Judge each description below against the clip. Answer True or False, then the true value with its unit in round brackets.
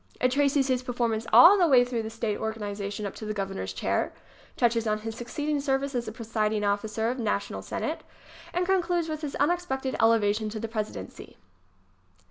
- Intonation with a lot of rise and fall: False (4.2 semitones)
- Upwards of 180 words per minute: True (190 wpm)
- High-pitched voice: True (230 Hz)